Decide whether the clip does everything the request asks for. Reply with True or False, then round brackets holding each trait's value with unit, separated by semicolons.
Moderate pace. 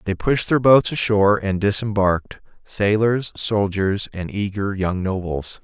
False (130 wpm)